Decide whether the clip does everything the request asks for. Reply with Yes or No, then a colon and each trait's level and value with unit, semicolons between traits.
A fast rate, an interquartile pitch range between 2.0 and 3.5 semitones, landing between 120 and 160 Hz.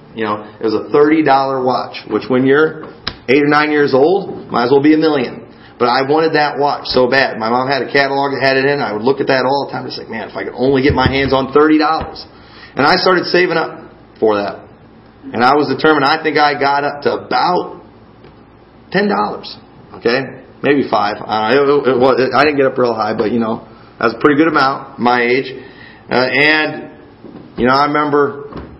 Yes: fast, 225 wpm; average, 3.0 semitones; medium, 140 Hz